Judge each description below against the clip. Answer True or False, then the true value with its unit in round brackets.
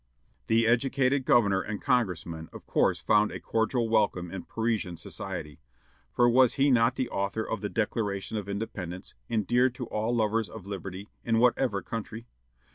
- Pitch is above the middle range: False (110 Hz)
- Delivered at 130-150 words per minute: False (160 wpm)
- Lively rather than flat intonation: False (3.3 semitones)